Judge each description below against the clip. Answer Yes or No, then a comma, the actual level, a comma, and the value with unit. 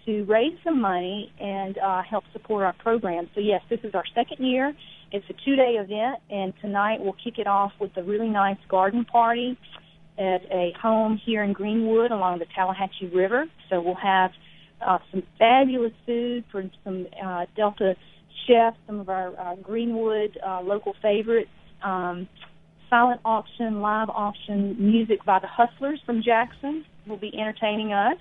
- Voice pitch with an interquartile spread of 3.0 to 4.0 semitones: Yes, average, 3.3 semitones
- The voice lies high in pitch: Yes, high, 210 Hz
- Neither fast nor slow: Yes, average, 170 wpm